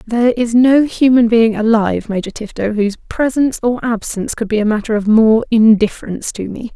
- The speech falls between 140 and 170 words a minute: No, average, 185 wpm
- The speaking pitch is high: Yes, high, 225 Hz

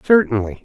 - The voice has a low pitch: Yes, low, 120 Hz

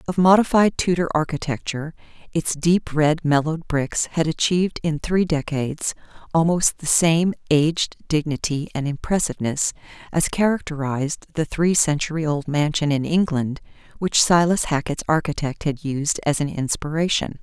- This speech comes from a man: No, female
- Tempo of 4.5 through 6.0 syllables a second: Yes, 5.0 syllables/s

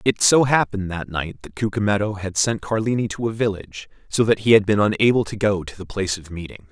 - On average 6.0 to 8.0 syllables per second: Yes, 6.1 syllables/s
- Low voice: Yes, low, 100 Hz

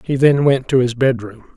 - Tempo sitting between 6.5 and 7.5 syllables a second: No, 4.9 syllables/s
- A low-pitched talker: Yes, low, 130 Hz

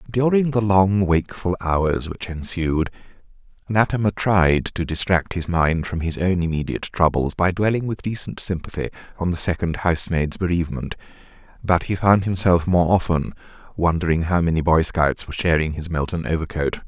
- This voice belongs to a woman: No, male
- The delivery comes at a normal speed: Yes, average, 155 wpm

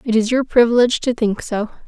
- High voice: Yes, high, 230 Hz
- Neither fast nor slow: No, fast, 225 wpm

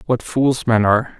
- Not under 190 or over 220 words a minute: Yes, average, 200 wpm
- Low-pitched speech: Yes, low, 120 Hz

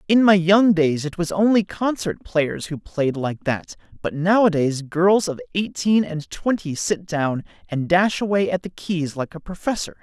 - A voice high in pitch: No, medium, 175 Hz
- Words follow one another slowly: No, average, 185 wpm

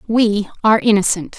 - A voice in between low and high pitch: No, high, 210 Hz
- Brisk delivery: No, slow, 130 wpm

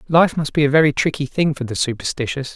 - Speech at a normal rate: No, fast, 235 wpm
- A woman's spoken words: No, male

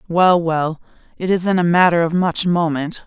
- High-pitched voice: No, medium, 170 Hz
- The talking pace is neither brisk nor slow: Yes, average, 175 wpm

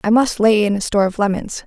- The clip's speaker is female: Yes, female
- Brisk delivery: Yes, fast, 290 wpm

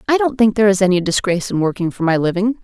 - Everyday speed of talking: No, fast, 275 wpm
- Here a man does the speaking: No, female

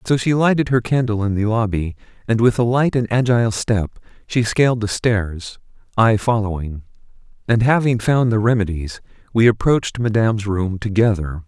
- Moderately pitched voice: No, low, 110 Hz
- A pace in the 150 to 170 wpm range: Yes, average, 160 wpm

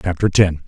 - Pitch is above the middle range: No, very low, 90 Hz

